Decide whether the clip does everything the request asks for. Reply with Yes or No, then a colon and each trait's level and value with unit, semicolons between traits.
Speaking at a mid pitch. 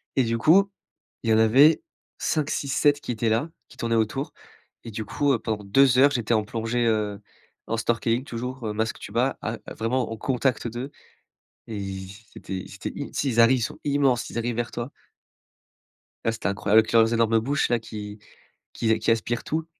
No: low, 115 Hz